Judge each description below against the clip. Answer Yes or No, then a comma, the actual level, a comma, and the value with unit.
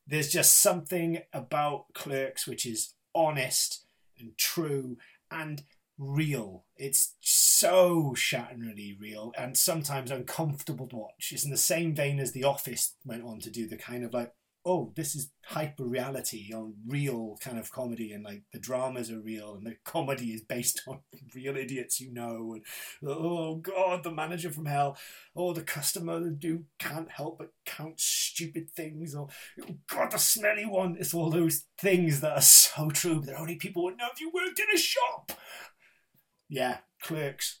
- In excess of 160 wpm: Yes, average, 170 wpm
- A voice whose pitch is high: No, medium, 145 Hz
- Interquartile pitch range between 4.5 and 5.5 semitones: Yes, average, 5.1 semitones